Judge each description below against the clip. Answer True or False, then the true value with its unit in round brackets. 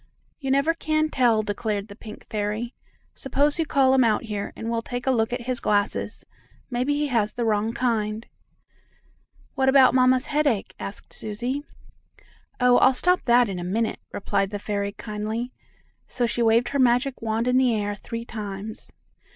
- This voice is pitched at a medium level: False (235 Hz)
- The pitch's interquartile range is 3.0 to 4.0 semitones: True (3.4 semitones)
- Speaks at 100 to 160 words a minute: False (175 wpm)